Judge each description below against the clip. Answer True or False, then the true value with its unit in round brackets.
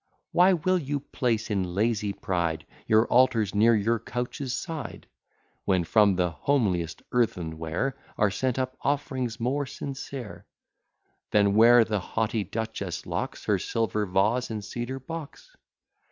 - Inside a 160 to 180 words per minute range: False (140 wpm)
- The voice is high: False (115 Hz)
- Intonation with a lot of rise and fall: False (4.6 semitones)